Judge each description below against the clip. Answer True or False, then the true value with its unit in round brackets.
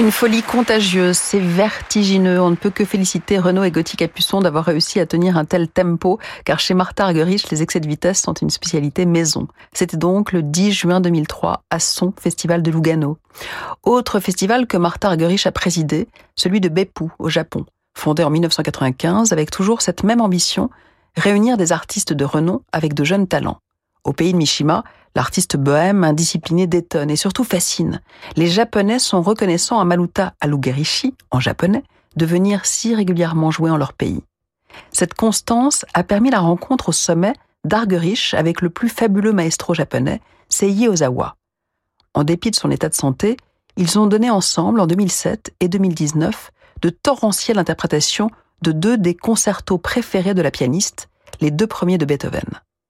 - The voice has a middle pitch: True (180 Hz)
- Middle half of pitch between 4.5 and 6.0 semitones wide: False (3.9 semitones)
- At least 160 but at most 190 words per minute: True (170 wpm)